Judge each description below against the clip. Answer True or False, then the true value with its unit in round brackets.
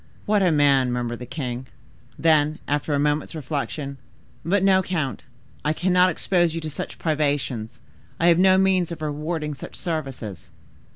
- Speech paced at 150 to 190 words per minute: True (155 wpm)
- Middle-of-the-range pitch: True (150 Hz)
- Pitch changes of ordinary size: True (4.0 semitones)